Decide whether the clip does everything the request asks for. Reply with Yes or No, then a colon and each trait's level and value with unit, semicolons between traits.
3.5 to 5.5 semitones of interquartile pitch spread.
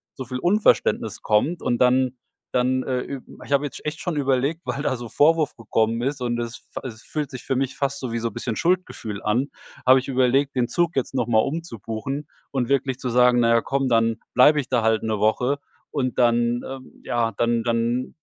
No: average, 2.9 semitones